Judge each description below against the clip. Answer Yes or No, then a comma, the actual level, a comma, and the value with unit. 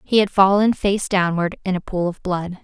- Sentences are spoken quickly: Yes, fast, 230 wpm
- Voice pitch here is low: No, high, 190 Hz